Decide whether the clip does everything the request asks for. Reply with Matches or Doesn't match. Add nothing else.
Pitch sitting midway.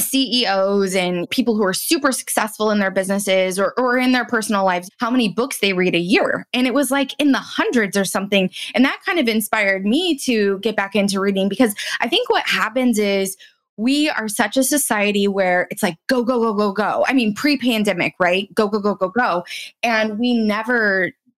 Doesn't match